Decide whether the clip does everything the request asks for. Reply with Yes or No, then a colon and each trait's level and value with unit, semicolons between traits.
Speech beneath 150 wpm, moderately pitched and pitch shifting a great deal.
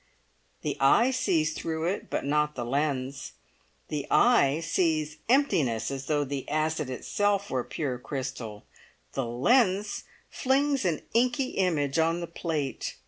Yes: average, 140 wpm; medium, 155 Hz; wide, 6.1 semitones